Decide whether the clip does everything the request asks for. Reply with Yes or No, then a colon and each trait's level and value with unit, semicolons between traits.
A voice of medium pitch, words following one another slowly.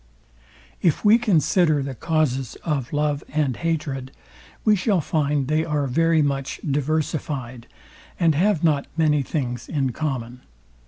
Yes: medium, 150 Hz; slow, 130 wpm